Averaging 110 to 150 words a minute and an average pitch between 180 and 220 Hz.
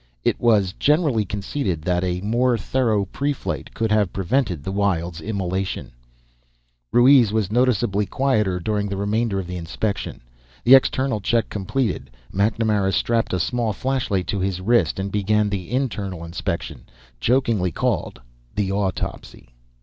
No: average, 140 wpm; low, 105 Hz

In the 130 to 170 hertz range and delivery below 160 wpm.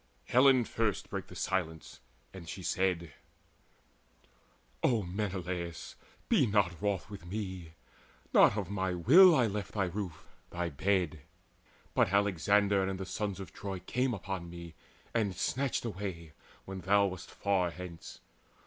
No: very low, 95 Hz; average, 140 wpm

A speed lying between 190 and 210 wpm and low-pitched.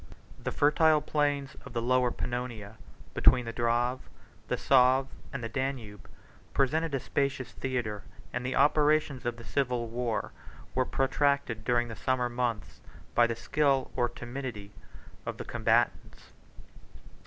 No: average, 140 wpm; low, 125 Hz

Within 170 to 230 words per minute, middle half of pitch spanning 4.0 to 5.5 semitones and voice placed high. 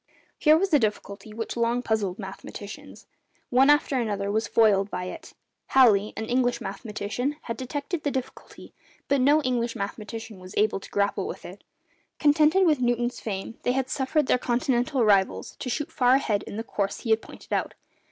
Yes: average, 180 wpm; average, 4.3 semitones; high, 235 Hz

